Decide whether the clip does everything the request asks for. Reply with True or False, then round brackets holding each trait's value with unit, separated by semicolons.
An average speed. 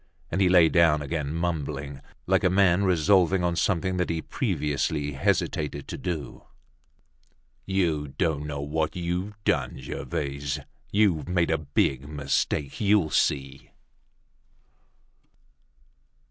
False (120 wpm)